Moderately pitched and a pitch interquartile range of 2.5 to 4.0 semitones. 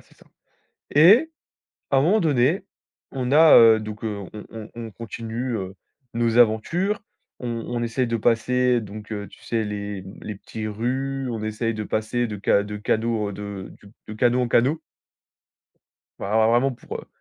No: low, 115 Hz; average, 2.9 semitones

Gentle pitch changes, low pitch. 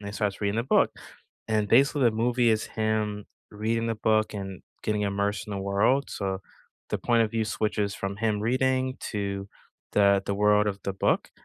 Yes: narrow, 2.1 semitones; low, 105 Hz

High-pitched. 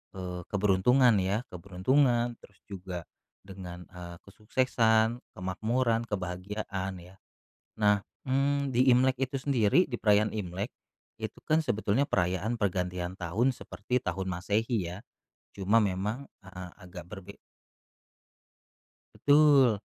No: low, 105 Hz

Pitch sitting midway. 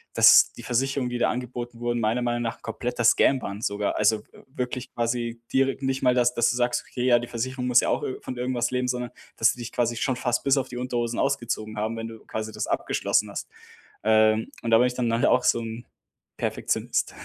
No: low, 120 Hz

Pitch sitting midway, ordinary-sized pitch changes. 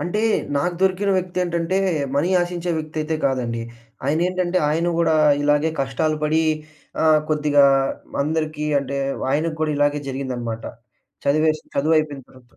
Yes: medium, 155 Hz; average, 3.1 semitones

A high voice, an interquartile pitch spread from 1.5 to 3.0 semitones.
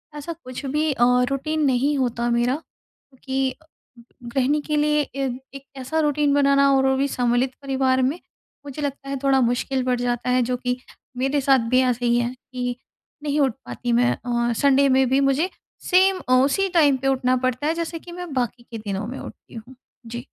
Yes: very high, 265 Hz; narrow, 2.4 semitones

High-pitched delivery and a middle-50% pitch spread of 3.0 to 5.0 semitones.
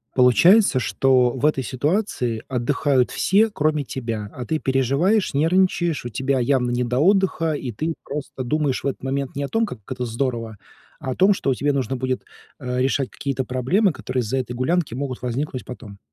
No: low, 135 Hz; average, 3.5 semitones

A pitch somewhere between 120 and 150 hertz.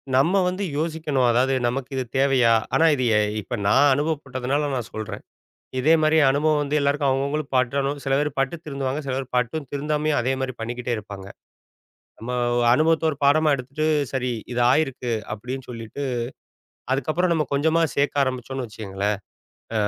Yes: low, 135 Hz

